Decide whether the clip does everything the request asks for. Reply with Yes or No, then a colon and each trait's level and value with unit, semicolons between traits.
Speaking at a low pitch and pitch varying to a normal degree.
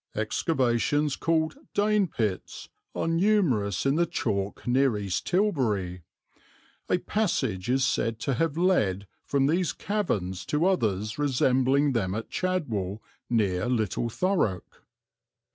No: low, 130 Hz; wide, 8.0 semitones